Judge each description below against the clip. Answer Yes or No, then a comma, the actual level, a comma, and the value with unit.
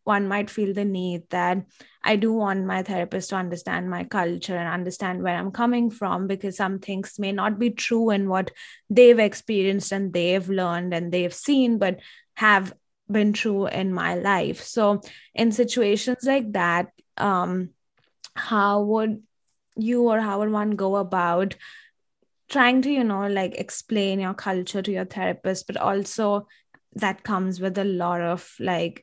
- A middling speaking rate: Yes, average, 165 wpm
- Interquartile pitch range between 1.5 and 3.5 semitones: Yes, narrow, 2.6 semitones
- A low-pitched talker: No, high, 195 Hz